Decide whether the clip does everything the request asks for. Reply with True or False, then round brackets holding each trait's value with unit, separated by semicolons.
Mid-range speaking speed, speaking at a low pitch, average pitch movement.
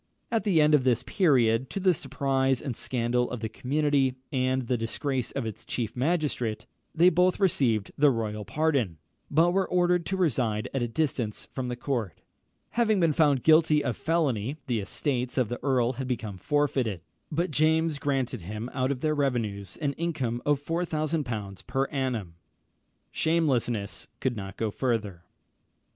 True (165 wpm; 130 Hz; 4.9 semitones)